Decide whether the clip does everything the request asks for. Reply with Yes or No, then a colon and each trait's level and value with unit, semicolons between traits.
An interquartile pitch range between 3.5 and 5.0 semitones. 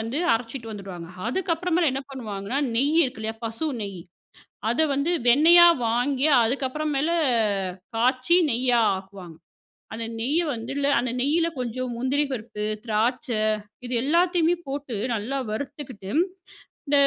Yes: average, 4.6 semitones